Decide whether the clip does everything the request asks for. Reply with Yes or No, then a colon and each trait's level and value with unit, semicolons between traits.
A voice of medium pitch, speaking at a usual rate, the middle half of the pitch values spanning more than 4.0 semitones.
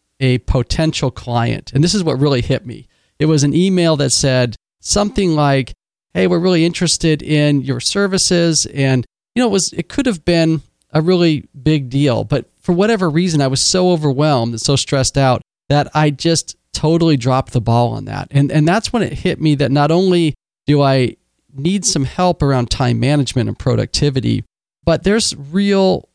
Yes: medium, 145 Hz; average, 195 wpm; average, 4.5 semitones